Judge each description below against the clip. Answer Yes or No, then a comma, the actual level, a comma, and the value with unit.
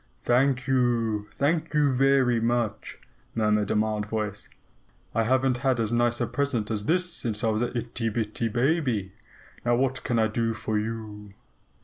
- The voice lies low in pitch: Yes, low, 115 Hz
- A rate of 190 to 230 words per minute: No, average, 165 wpm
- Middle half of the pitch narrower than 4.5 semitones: Yes, average, 3.2 semitones